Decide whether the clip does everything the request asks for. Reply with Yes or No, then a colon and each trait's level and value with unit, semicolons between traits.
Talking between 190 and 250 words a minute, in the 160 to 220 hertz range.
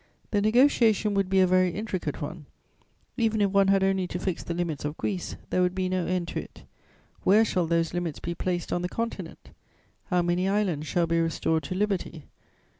Yes: average, 200 wpm; medium, 185 Hz